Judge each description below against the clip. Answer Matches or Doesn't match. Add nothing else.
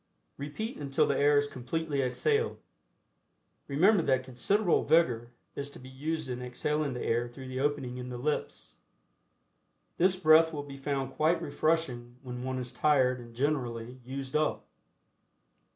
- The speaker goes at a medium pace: Matches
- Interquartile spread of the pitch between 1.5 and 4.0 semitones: Matches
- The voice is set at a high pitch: Doesn't match